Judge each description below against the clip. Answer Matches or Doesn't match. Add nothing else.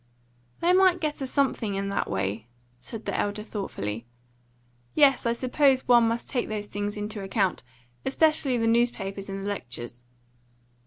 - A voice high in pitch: Matches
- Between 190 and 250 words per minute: Doesn't match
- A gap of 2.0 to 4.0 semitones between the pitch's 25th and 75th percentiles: Doesn't match